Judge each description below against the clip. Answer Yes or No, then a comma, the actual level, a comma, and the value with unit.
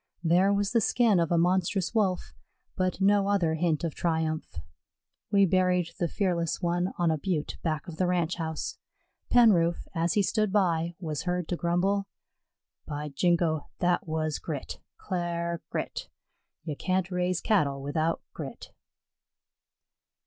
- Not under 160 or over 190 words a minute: No, average, 145 wpm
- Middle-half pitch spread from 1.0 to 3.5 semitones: Yes, narrow, 2.6 semitones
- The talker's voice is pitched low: No, medium, 175 Hz